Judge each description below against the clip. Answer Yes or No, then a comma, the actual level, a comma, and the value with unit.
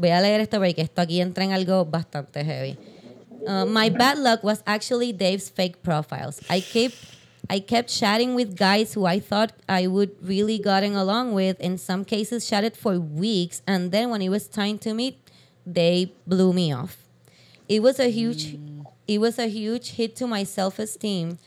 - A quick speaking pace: No, average, 150 wpm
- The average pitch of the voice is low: No, high, 195 Hz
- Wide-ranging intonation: No, average, 3.4 semitones